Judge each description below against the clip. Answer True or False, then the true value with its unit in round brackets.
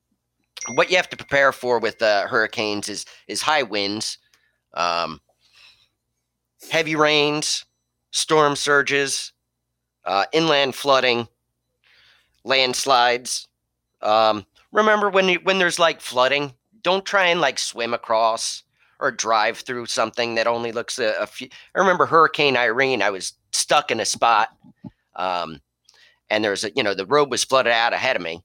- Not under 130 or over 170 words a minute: True (145 wpm)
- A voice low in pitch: True (120 Hz)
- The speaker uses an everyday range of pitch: False (6.3 semitones)